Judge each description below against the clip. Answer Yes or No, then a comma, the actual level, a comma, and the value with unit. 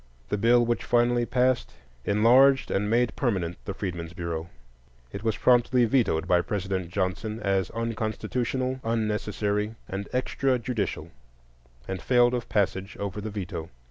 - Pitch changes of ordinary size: Yes, average, 4.0 semitones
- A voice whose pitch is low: Yes, low, 110 Hz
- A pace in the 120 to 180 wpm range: Yes, slow, 135 wpm